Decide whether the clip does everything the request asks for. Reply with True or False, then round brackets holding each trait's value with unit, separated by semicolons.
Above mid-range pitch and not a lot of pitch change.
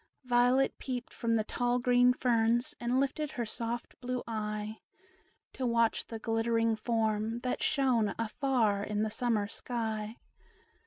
True (235 Hz; 2.0 semitones)